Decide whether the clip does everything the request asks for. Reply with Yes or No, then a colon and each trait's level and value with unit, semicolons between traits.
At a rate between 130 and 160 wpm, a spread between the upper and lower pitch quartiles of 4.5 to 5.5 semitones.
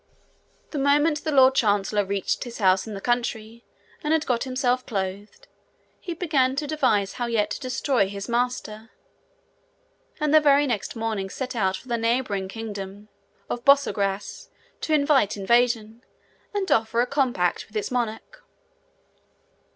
Yes: average, 150 wpm; average, 4.8 semitones